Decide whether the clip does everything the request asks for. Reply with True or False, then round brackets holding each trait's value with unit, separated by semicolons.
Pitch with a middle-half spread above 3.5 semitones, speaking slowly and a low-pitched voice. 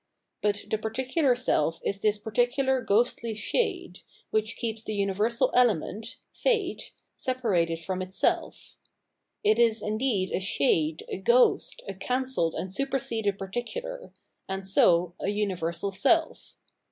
False (4.6 semitones; 125 wpm; 215 Hz)